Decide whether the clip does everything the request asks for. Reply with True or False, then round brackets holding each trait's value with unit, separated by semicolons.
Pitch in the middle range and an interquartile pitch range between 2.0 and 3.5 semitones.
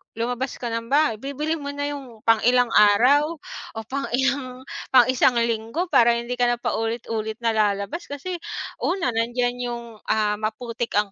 False (240 Hz; 3.1 semitones)